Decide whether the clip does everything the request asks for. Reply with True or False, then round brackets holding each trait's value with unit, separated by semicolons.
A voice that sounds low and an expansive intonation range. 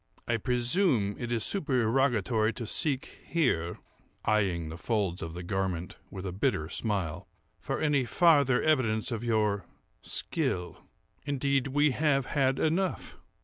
True (120 Hz; 5.8 semitones)